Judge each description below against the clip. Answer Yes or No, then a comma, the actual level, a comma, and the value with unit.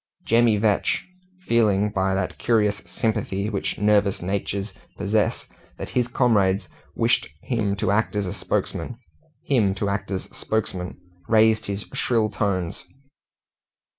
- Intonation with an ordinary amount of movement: No, narrow, 2.2 semitones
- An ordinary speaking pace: No, slow, 105 wpm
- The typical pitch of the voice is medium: No, low, 105 Hz